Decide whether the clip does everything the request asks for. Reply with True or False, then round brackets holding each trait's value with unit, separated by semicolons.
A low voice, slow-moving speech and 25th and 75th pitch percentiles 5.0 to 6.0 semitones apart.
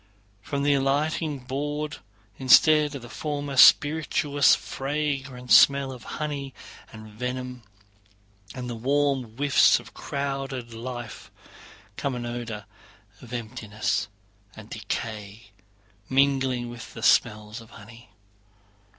False (130 Hz; 110 wpm; 3.2 semitones)